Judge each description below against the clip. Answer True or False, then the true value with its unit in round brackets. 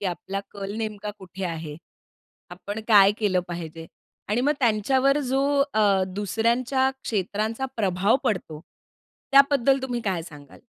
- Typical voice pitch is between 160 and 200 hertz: False (210 Hz)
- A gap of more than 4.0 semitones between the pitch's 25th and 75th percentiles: True (4.8 semitones)